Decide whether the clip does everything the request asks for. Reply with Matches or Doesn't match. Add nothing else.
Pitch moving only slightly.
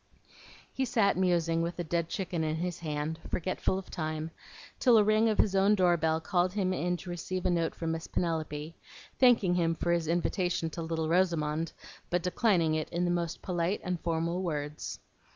Matches